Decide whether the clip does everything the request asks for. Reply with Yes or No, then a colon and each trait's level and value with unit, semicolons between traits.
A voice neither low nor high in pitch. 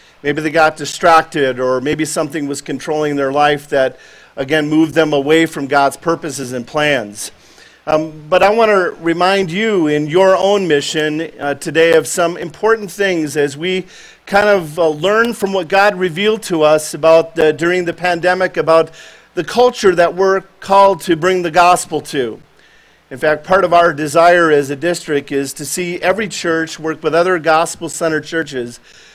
Yes: medium, 165 Hz